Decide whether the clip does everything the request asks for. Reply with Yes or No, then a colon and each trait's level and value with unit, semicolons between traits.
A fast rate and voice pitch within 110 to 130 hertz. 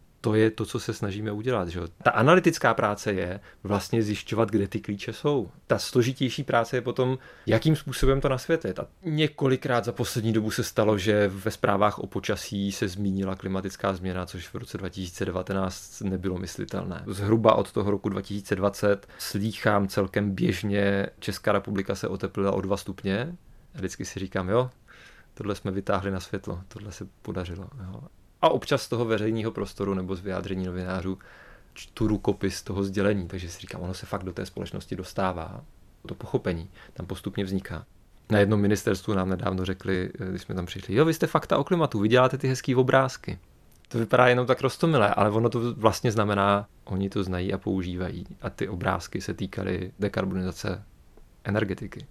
No: fast, 175 wpm; low, 100 Hz